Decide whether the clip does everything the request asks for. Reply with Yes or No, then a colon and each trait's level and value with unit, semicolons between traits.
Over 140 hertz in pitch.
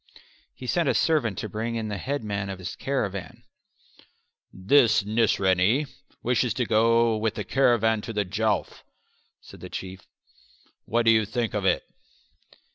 No: low, 110 Hz